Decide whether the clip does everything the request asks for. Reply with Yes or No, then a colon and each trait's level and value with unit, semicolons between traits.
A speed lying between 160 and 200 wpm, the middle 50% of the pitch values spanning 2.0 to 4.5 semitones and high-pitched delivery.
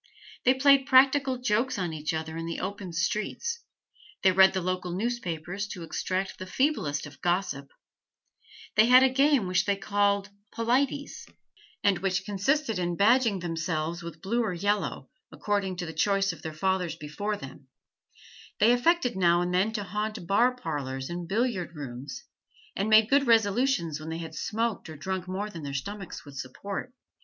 No: average, 170 wpm; average, 5.1 semitones; high, 195 Hz